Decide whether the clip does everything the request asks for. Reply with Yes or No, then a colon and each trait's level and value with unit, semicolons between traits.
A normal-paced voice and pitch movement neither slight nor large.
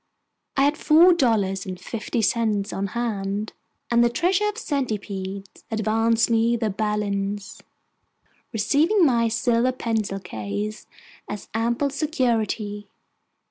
No: slow, 120 wpm; average, 3.5 semitones